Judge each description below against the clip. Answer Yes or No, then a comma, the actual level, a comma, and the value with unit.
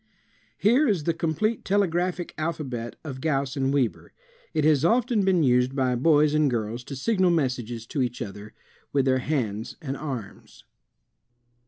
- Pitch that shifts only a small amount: No, average, 5.0 semitones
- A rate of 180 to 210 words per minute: No, average, 155 wpm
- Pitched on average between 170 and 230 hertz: No, medium, 145 Hz